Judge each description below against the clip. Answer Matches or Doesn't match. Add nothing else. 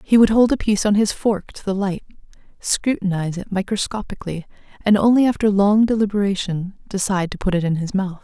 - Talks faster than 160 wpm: Matches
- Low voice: Doesn't match